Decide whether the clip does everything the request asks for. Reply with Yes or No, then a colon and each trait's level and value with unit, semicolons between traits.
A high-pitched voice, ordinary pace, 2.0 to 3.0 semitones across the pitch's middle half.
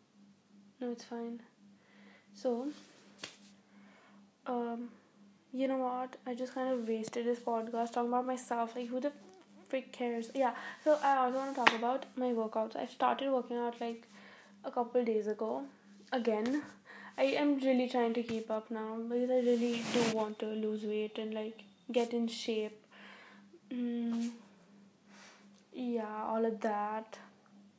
Yes: high, 235 Hz; average, 150 wpm; narrow, 2.5 semitones